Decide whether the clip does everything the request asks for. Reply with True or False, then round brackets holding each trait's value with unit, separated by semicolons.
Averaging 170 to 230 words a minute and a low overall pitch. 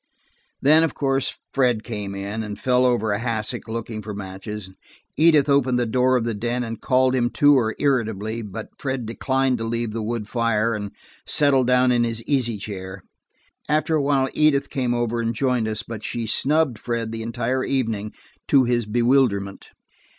True (180 wpm; 120 Hz)